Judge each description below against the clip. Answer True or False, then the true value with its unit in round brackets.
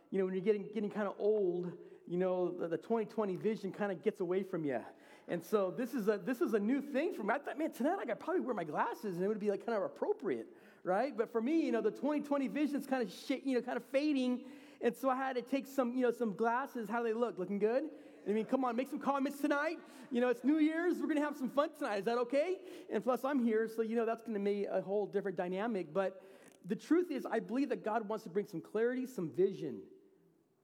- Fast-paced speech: True (265 wpm)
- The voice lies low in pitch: False (235 Hz)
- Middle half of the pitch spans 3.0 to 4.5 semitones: False (5.0 semitones)